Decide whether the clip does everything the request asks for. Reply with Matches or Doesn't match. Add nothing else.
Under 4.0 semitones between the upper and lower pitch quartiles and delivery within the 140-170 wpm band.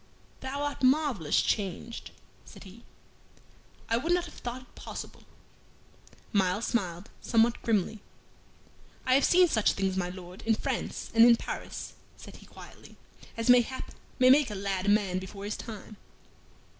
Doesn't match